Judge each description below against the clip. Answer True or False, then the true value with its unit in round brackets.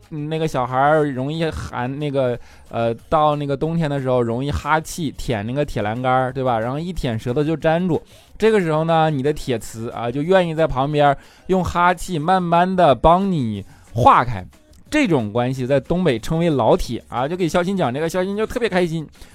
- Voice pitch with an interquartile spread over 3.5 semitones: True (5.1 semitones)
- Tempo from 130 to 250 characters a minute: False (285 characters per minute)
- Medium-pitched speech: True (150 Hz)